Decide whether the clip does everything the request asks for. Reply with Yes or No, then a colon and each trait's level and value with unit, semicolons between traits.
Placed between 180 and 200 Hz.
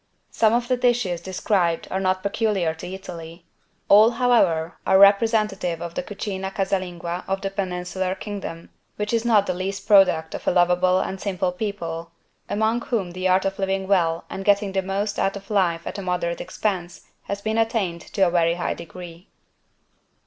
Yes: high, 190 Hz